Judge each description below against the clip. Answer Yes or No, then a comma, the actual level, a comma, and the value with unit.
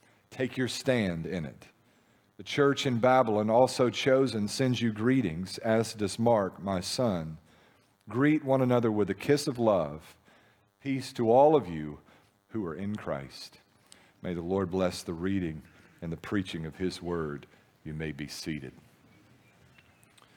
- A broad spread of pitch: Yes, wide, 6.3 semitones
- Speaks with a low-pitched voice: Yes, low, 105 Hz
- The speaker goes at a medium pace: Yes, average, 155 wpm